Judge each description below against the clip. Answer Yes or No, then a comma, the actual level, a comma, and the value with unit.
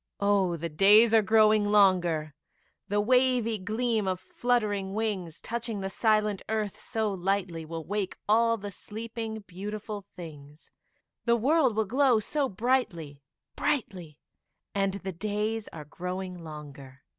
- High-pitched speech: Yes, high, 205 Hz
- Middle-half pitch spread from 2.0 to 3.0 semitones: No, average, 3.6 semitones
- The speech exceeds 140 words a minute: No, slow, 135 wpm